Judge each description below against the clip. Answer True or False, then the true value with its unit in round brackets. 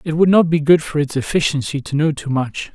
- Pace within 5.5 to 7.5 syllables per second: True (5.7 syllables/s)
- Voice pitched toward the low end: False (150 Hz)